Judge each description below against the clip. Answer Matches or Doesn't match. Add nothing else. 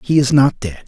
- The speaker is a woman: Doesn't match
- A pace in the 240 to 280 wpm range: Matches